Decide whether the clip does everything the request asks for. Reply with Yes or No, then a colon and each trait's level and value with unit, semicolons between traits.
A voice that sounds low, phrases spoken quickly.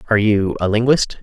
No: low, 110 Hz; average, 195 wpm